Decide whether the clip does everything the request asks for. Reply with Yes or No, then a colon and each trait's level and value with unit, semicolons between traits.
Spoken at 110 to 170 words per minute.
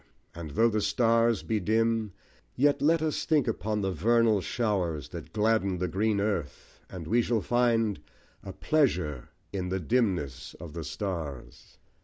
Yes: average, 155 wpm